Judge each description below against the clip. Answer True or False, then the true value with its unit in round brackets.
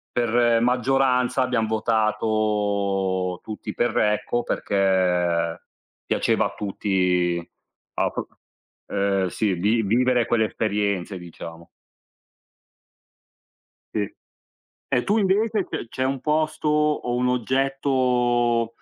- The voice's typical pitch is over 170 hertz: False (110 Hz)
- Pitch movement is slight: False (4.3 semitones)